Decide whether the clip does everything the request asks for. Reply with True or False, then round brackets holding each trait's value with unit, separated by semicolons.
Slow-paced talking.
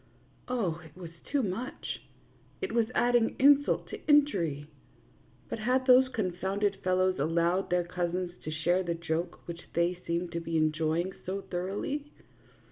False (150 wpm)